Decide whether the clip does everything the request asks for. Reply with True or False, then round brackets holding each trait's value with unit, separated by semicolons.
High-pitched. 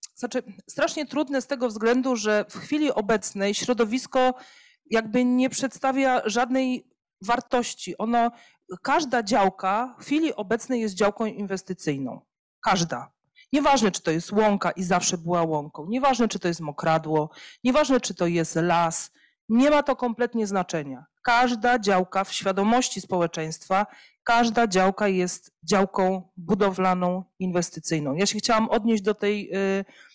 True (210 Hz)